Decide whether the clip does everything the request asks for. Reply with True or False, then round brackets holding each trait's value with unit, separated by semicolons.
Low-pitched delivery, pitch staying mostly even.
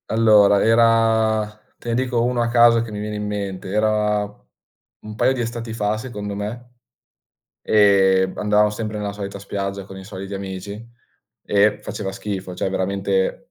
True (105 Hz; 2.3 semitones)